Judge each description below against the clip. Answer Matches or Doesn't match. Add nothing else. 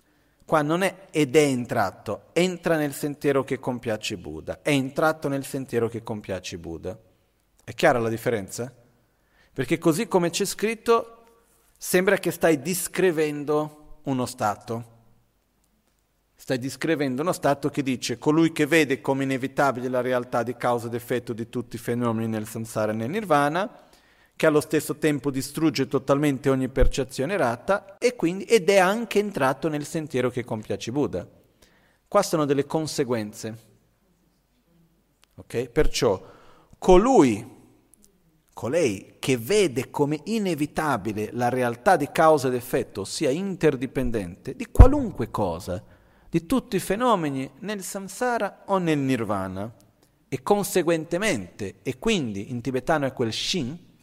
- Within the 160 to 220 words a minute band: Doesn't match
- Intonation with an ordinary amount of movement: Doesn't match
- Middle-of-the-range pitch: Matches